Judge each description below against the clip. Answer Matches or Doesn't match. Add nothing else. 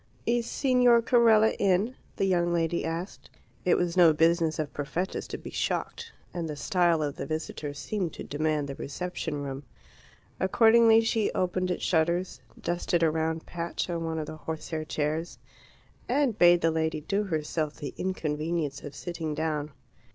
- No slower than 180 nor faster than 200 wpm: Doesn't match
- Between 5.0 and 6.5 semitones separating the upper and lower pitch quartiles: Doesn't match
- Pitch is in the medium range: Matches